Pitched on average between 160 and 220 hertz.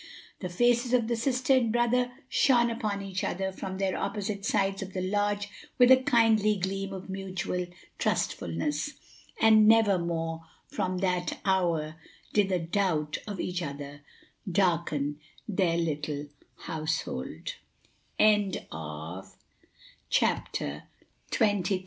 Yes: high, 190 Hz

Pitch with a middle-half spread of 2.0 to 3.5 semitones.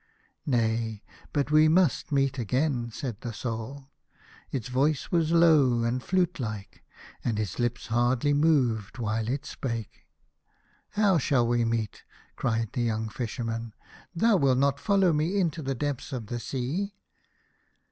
No: average, 4.6 semitones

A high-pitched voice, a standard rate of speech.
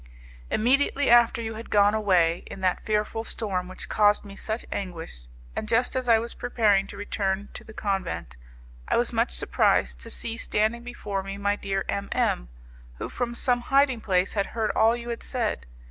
Yes: high, 210 Hz; average, 190 wpm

